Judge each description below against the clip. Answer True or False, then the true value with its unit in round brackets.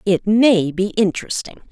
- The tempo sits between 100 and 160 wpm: True (140 wpm)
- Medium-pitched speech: False (200 Hz)